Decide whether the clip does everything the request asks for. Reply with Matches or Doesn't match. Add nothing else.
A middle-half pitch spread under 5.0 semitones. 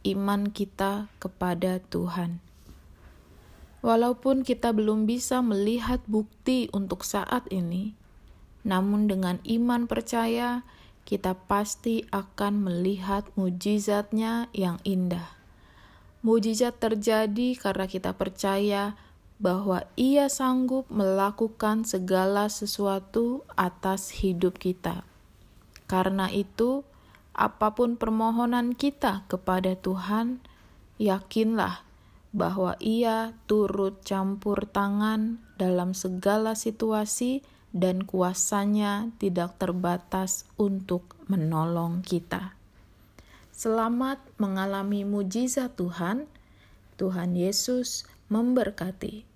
Matches